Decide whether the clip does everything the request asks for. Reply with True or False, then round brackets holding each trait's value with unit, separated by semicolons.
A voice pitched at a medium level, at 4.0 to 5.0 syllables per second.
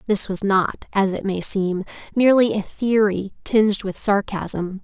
False (200 Hz; 4.3 syllables/s)